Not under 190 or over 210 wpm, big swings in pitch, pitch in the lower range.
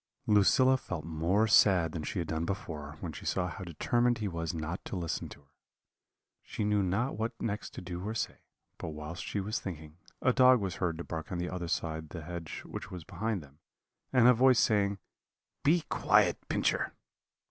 No: average, 200 wpm; average, 4.7 semitones; very low, 90 Hz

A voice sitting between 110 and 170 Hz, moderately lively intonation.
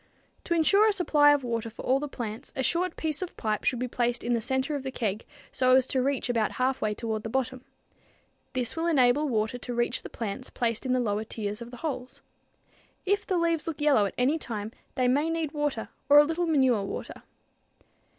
No: very high, 255 Hz; average, 4.2 semitones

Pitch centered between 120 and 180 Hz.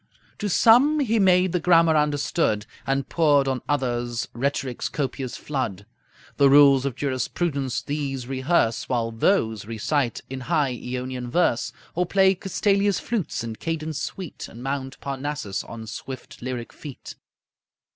Yes: medium, 140 Hz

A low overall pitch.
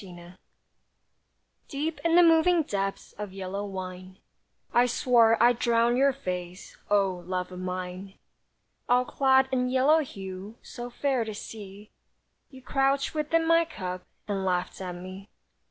No: high, 215 Hz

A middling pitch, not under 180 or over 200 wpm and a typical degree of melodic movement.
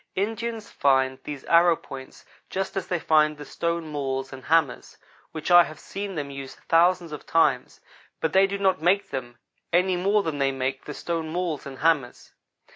Yes: medium, 160 Hz; average, 185 wpm; average, 4.7 semitones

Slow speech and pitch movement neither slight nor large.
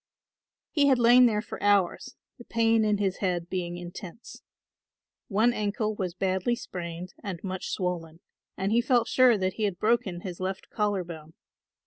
No: average, 165 wpm; average, 4.1 semitones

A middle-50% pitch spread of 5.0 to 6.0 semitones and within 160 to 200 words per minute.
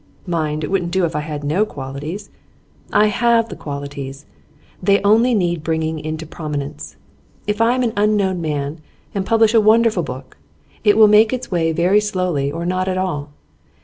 Yes: wide, 5.6 semitones; average, 180 wpm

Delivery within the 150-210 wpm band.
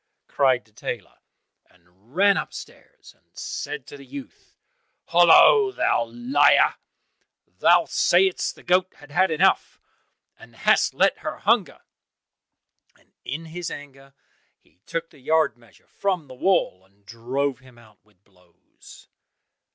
No: slow, 135 wpm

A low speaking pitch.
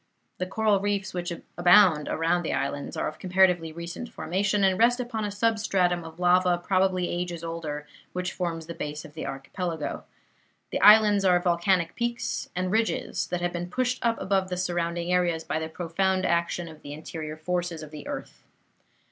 No: medium, 180 Hz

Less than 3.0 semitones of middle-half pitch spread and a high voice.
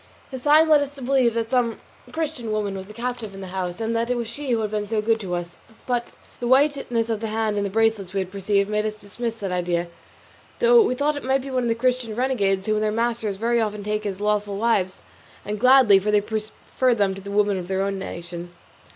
No: average, 3.4 semitones; high, 215 Hz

